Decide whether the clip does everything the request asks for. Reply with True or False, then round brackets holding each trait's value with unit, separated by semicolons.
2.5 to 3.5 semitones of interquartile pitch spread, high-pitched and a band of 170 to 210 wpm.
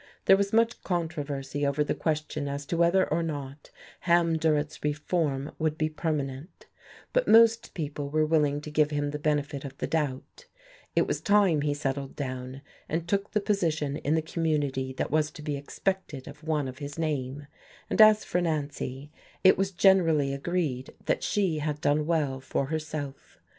False (2.9 semitones; 150 Hz; 175 wpm)